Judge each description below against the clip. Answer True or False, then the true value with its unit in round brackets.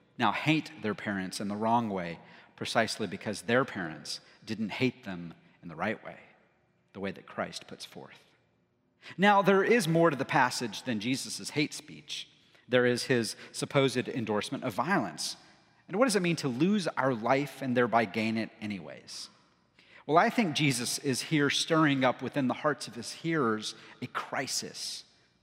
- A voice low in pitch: True (130 Hz)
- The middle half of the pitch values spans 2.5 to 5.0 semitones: False (5.4 semitones)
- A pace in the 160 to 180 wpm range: True (170 wpm)